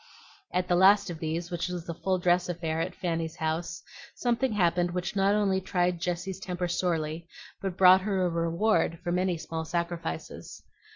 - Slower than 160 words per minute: No, average, 175 wpm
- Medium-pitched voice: Yes, medium, 175 Hz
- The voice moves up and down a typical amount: No, narrow, 1.9 semitones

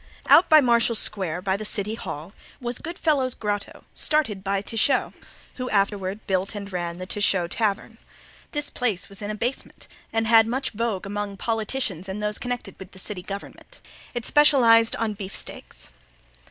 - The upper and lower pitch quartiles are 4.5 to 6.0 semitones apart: No, average, 3.5 semitones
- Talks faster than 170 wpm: No, average, 165 wpm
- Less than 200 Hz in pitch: No, high, 210 Hz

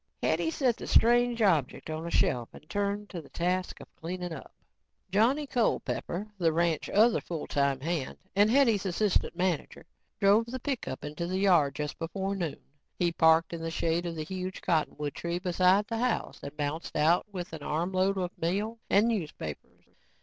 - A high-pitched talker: No, medium, 180 Hz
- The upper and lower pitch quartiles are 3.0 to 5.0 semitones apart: Yes, average, 4.1 semitones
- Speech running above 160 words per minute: Yes, average, 180 wpm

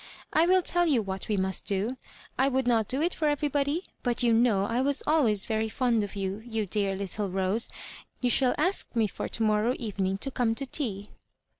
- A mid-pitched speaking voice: No, high, 230 Hz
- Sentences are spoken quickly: Yes, fast, 210 wpm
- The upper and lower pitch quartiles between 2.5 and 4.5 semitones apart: No, average, 5.0 semitones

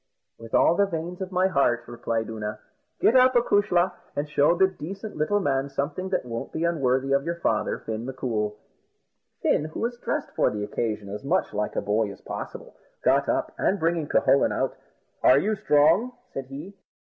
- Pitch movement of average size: No, wide, 7.7 semitones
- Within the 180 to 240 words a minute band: Yes, average, 185 wpm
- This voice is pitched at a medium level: Yes, medium, 145 Hz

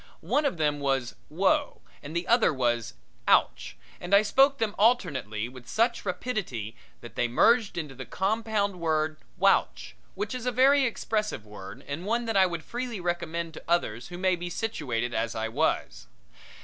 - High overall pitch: No, medium, 175 Hz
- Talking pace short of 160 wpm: No, average, 175 wpm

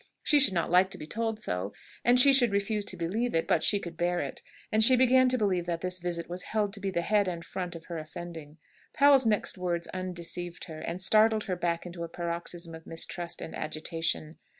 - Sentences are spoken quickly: Yes, fast, 225 wpm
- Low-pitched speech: No, medium, 180 Hz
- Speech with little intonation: No, average, 4.1 semitones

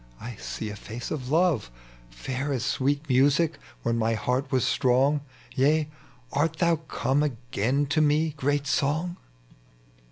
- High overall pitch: No, medium, 140 Hz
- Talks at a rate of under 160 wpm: Yes, average, 150 wpm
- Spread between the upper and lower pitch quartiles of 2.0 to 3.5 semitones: Yes, average, 3.2 semitones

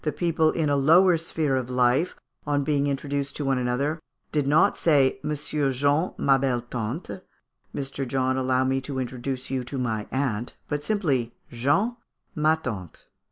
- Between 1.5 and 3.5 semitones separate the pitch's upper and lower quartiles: Yes, average, 2.9 semitones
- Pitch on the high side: No, low, 135 Hz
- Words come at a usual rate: Yes, average, 160 wpm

